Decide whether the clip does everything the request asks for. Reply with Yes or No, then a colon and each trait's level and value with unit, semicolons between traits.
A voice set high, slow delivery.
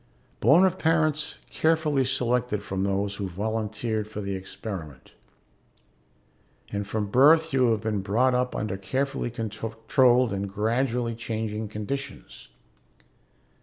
No: low, 115 Hz; slow, 120 wpm